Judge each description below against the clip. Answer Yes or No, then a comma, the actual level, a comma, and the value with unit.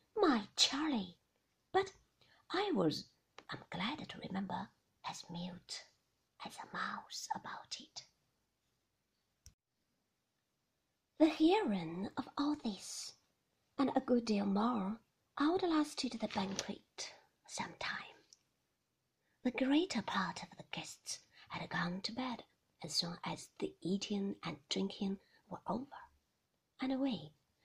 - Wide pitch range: Yes, wide, 7.1 semitones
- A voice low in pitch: No, high, 230 Hz